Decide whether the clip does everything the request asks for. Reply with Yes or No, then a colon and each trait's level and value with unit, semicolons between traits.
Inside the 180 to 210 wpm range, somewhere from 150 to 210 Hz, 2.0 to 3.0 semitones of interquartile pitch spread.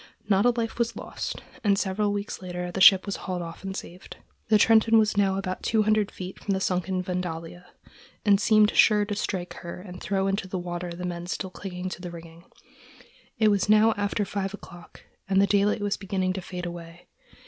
Yes: fast, 205 wpm; high, 190 Hz; narrow, 2.4 semitones